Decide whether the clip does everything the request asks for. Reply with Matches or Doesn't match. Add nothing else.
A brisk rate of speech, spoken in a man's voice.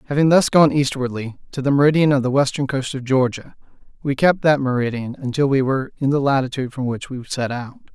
Matches